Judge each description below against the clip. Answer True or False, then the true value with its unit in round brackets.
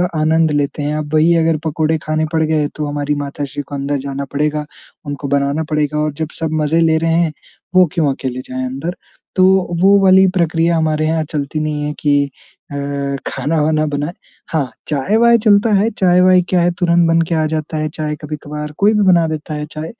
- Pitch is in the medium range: True (155 Hz)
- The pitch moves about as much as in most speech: False (2.0 semitones)